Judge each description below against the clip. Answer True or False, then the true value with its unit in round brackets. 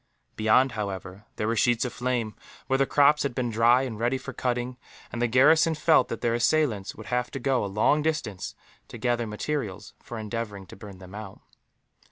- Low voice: True (120 Hz)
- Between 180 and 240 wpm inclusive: True (200 wpm)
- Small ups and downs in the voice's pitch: False (3.7 semitones)